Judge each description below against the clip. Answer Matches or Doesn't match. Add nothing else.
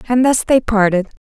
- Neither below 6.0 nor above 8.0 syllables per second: Doesn't match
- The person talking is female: Matches